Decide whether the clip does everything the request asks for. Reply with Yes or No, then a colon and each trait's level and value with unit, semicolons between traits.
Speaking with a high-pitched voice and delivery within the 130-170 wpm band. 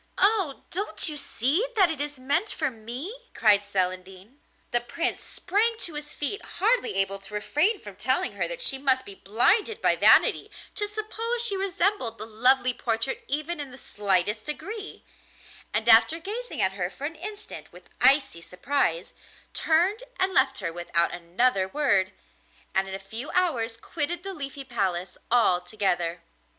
Yes: very high, 265 Hz; average, 160 wpm